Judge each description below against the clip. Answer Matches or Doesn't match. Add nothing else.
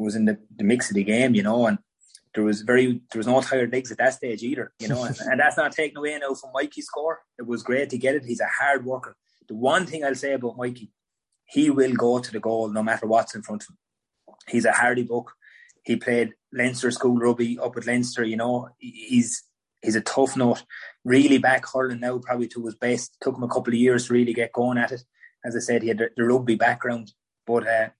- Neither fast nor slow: Doesn't match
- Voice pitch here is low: Matches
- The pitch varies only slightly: Matches